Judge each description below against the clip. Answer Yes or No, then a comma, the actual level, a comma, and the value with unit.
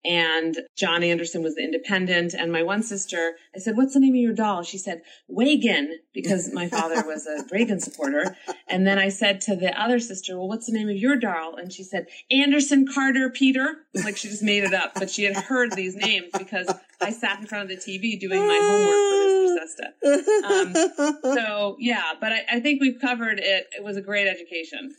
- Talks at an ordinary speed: No, fast, 215 wpm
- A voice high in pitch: Yes, high, 205 Hz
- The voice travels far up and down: Yes, wide, 5.8 semitones